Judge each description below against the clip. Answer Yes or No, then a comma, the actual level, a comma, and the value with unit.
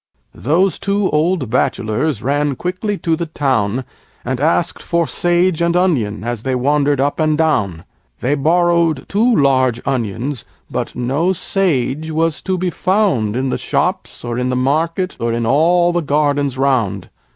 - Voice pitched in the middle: Yes, medium, 145 Hz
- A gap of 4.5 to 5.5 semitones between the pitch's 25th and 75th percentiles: Yes, average, 5.2 semitones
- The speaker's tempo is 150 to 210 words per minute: Yes, average, 160 wpm